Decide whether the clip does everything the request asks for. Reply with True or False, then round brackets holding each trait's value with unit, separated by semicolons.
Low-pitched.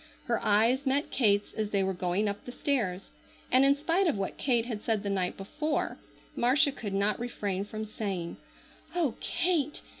False (220 Hz)